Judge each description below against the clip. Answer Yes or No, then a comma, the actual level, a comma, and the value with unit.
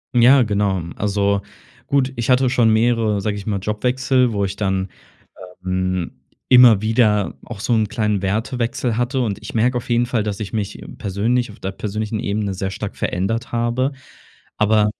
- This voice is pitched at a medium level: No, low, 110 Hz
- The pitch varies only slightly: No, average, 3.2 semitones